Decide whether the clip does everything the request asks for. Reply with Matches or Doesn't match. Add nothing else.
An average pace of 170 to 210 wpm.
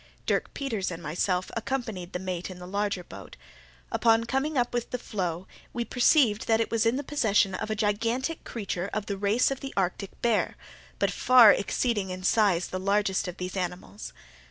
Matches